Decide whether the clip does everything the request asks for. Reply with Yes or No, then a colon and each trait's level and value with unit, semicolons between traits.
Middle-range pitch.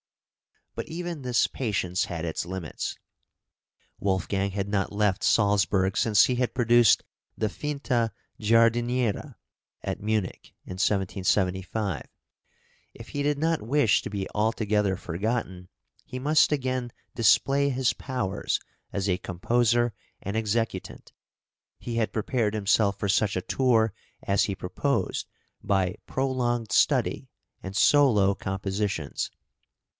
No: low, 105 Hz